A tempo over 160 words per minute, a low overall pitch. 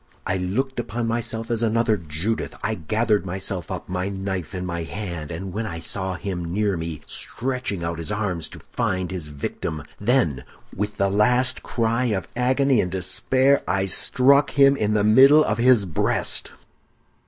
Yes: average, 170 wpm; low, 105 Hz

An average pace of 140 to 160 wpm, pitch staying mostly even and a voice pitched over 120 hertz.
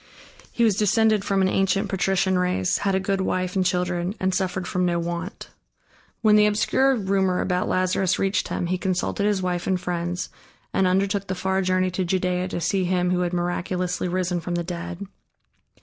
No: average, 190 wpm; narrow, 1.3 semitones; medium, 185 Hz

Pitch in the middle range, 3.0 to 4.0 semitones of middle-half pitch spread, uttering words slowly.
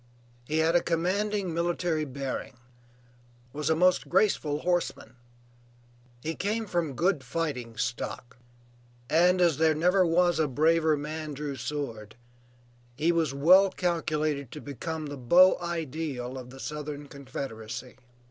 Yes: medium, 155 Hz; average, 3.7 semitones; slow, 130 wpm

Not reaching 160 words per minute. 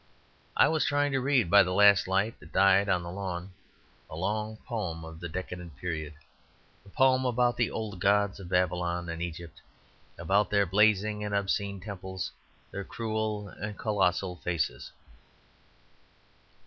Yes: average, 150 wpm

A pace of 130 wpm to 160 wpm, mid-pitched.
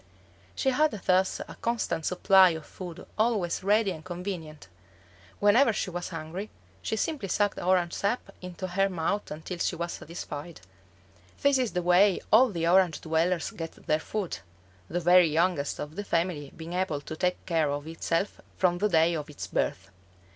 No: average, 170 wpm; medium, 180 Hz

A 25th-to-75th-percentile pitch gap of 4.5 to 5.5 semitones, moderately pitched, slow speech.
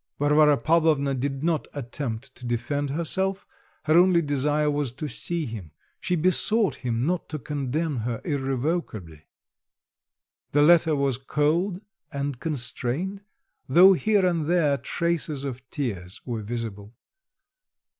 Yes: average, 4.9 semitones; medium, 145 Hz; slow, 125 wpm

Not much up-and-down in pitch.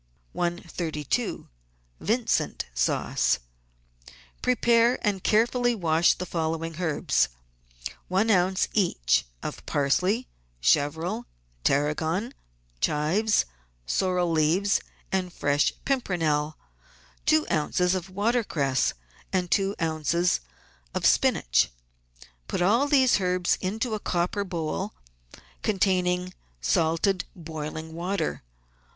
No: average, 4.3 semitones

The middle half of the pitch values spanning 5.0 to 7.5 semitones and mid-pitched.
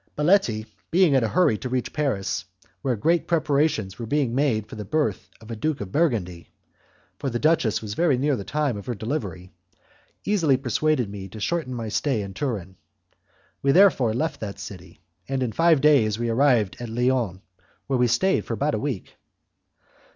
No: wide, 5.6 semitones; low, 125 Hz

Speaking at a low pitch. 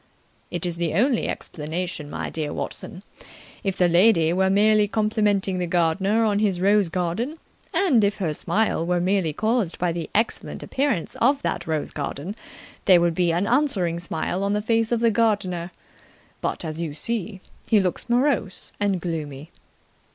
No: high, 190 Hz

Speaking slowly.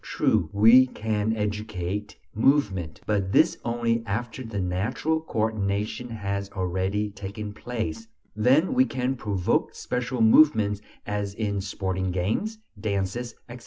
Yes: slow, 125 wpm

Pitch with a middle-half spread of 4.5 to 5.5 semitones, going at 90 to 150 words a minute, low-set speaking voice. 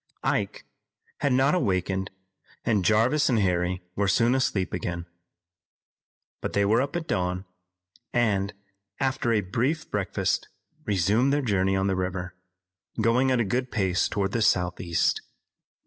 Yes: average, 5.1 semitones; average, 140 wpm; low, 100 Hz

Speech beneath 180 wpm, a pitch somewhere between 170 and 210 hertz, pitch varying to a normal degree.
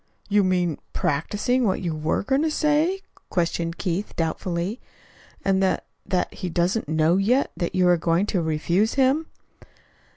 Yes: average, 155 wpm; medium, 185 Hz; average, 4.6 semitones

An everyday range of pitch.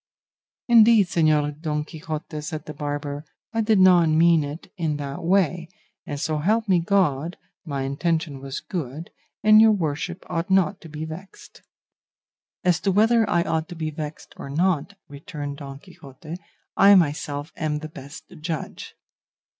Yes: average, 3.7 semitones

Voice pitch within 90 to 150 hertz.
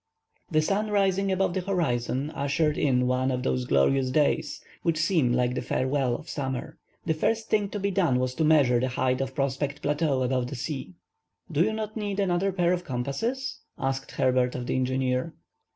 Yes: medium, 140 Hz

